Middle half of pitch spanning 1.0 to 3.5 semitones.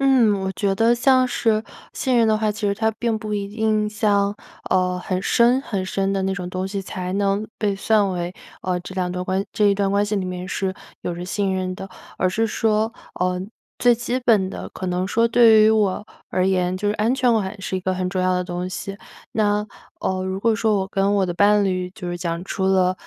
Yes: average, 2.7 semitones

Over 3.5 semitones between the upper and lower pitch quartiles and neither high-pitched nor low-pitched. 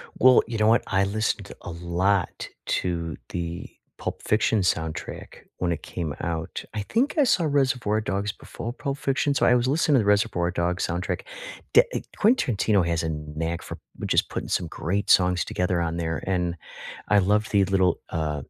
No: average, 4.7 semitones; very low, 95 Hz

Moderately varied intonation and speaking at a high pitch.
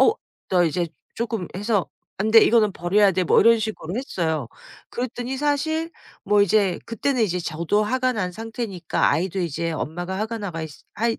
Yes: average, 4.6 semitones; high, 205 Hz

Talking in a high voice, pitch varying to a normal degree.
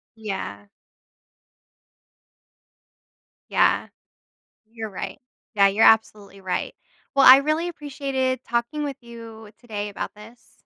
Yes: high, 230 Hz; average, 4.3 semitones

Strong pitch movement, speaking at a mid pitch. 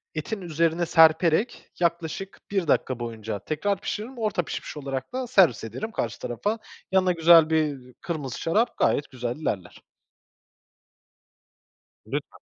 Yes: wide, 6.2 semitones; medium, 160 Hz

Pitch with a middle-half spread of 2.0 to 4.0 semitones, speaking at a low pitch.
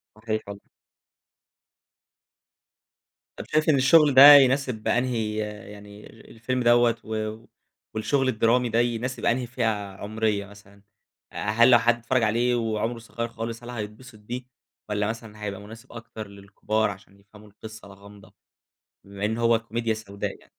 Yes: narrow, 2.4 semitones; low, 110 Hz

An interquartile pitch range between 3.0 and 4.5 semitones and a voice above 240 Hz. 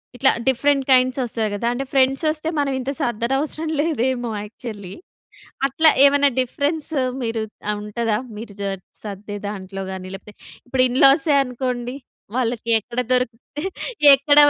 Yes: average, 3.9 semitones; very high, 250 Hz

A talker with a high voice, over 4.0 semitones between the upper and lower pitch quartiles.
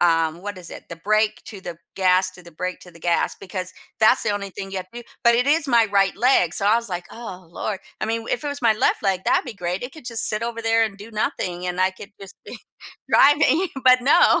Yes: high, 205 Hz; average, 4.4 semitones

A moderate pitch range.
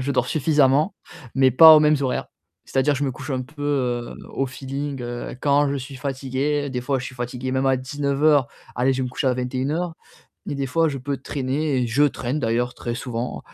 No: narrow, 2.2 semitones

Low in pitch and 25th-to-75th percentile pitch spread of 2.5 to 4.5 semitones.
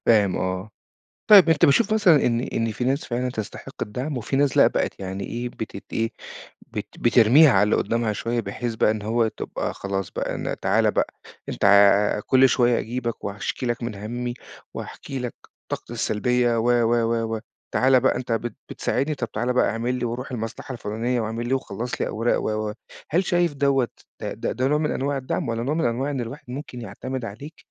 Yes: low, 120 Hz; average, 2.8 semitones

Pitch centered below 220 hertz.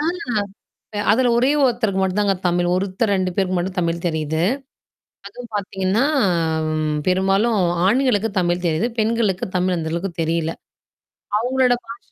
Yes: high, 190 Hz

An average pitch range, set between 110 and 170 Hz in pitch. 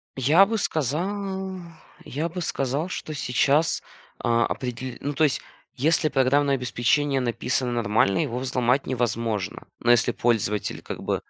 Yes: average, 4.2 semitones; low, 135 Hz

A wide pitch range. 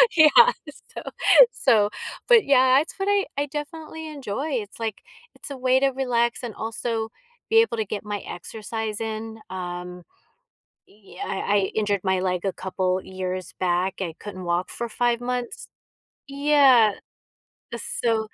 Yes: wide, 5.7 semitones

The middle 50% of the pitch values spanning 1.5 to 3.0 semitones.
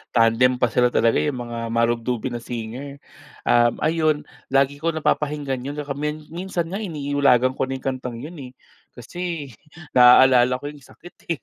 No: average, 3.5 semitones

